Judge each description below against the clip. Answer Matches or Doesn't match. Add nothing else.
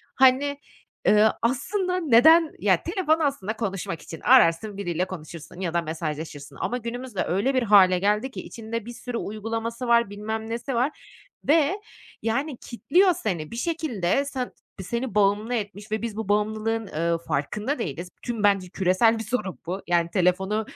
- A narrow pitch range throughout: Doesn't match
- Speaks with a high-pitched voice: Matches